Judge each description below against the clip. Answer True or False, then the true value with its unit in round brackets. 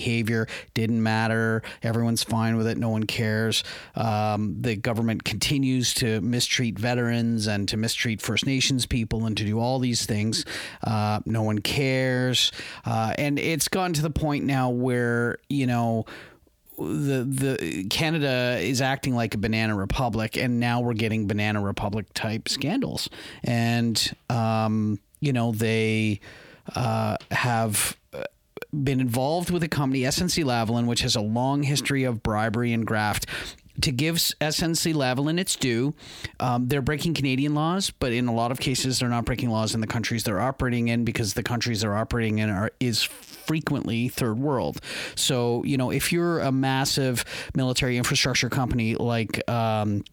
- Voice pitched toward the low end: True (120 Hz)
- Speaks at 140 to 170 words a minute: True (160 wpm)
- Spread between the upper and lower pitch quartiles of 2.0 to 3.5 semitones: True (3.1 semitones)